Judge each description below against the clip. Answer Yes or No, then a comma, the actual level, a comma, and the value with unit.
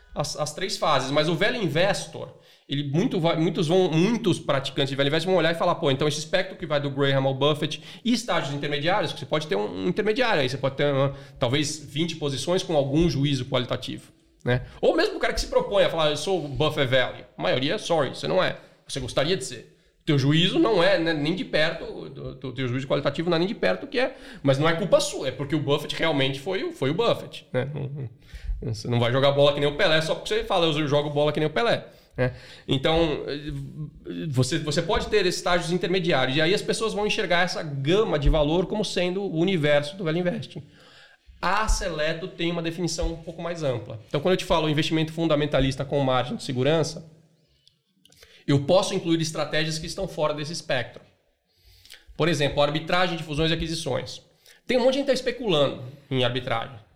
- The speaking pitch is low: No, medium, 155 Hz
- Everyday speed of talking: No, fast, 215 wpm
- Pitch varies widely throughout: No, average, 4.0 semitones